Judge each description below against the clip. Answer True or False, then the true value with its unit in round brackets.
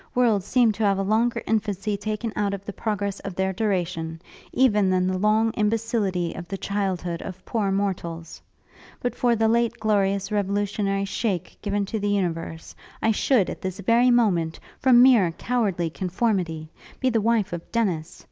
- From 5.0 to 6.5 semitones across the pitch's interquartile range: False (3.2 semitones)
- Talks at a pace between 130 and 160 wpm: False (170 wpm)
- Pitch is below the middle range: False (200 Hz)